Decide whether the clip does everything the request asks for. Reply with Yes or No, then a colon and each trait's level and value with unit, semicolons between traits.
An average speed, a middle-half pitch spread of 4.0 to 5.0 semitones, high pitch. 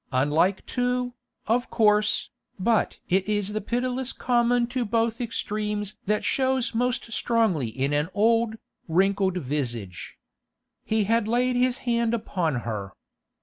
No: slow, 130 wpm; average, 4.5 semitones; high, 215 Hz